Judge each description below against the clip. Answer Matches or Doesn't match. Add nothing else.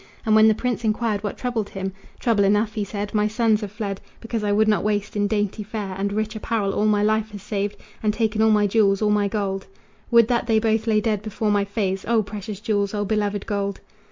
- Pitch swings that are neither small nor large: Doesn't match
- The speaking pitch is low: Doesn't match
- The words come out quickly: Matches